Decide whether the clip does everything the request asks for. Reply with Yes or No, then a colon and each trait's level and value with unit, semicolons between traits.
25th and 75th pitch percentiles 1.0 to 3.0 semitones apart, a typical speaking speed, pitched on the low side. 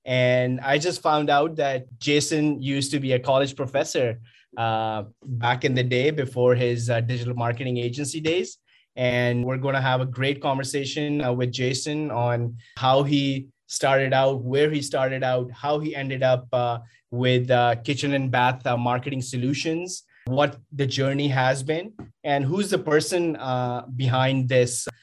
Yes: narrow, 2.5 semitones; average, 170 wpm; low, 130 Hz